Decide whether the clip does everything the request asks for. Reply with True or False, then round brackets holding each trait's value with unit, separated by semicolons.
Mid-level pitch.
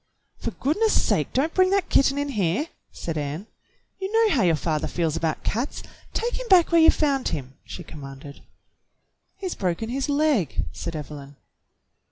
False (245 Hz)